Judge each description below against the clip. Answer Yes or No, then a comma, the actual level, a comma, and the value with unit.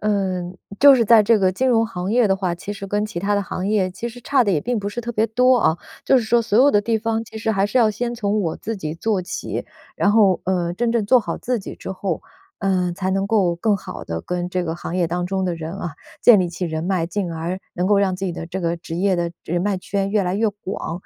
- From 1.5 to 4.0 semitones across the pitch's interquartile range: Yes, average, 3.7 semitones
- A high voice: Yes, high, 195 Hz